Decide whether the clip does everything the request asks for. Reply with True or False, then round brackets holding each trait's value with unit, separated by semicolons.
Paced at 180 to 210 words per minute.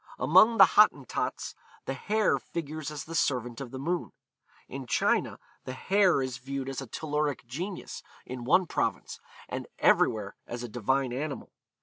False (155 wpm)